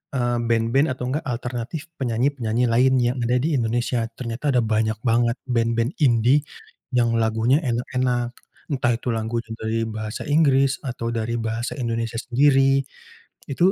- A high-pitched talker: No, low, 120 Hz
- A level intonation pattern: Yes, narrow, 2.2 semitones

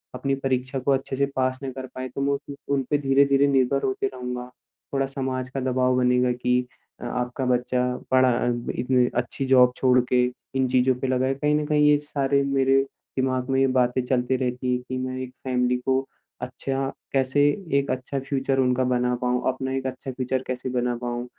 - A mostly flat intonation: Yes, narrow, 1.2 semitones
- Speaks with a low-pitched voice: Yes, low, 130 Hz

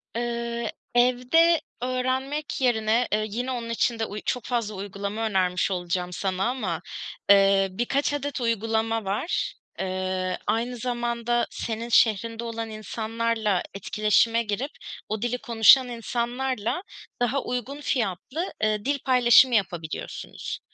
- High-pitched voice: Yes, high, 230 Hz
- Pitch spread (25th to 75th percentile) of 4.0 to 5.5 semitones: No, average, 3.2 semitones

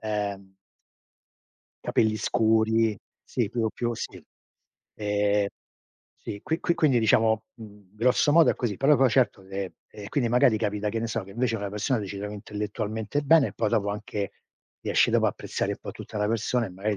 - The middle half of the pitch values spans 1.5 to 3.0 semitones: Yes, narrow, 2.4 semitones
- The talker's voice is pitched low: Yes, low, 110 Hz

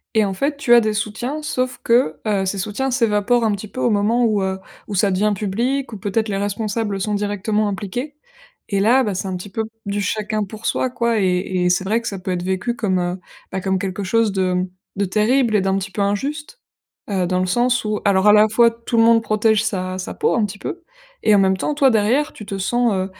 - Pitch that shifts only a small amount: No, average, 3.2 semitones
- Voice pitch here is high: Yes, high, 210 Hz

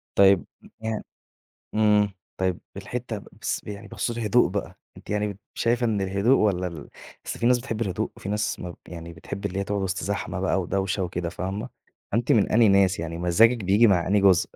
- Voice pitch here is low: Yes, low, 100 Hz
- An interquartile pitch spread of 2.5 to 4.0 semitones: Yes, average, 2.8 semitones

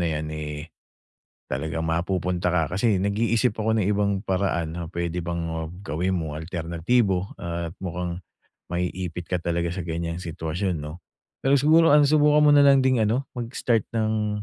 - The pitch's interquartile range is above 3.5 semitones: Yes, average, 4.5 semitones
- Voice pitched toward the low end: Yes, very low, 90 Hz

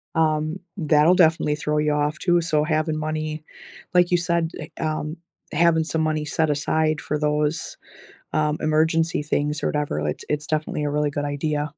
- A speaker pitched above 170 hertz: No, medium, 155 Hz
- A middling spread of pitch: No, narrow, 1.2 semitones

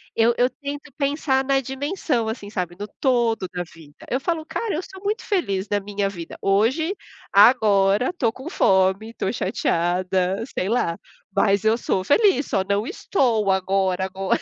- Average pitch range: No, wide, 6.0 semitones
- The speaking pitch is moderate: No, high, 220 Hz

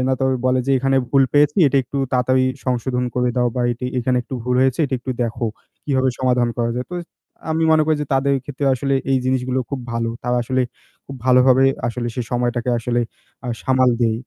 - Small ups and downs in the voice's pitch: Yes, narrow, 1.5 semitones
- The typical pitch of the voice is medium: No, low, 130 Hz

